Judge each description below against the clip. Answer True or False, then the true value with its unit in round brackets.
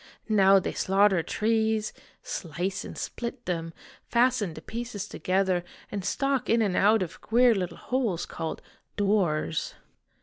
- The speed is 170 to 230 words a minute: False (140 wpm)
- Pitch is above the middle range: True (200 Hz)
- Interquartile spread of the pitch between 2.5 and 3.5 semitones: False (4.0 semitones)